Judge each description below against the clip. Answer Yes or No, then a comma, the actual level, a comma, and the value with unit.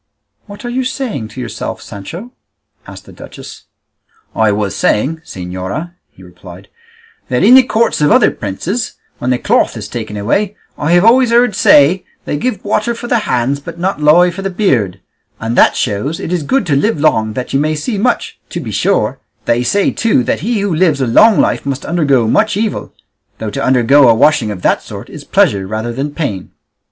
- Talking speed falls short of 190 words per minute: No, average, 200 wpm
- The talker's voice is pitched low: No, medium, 150 Hz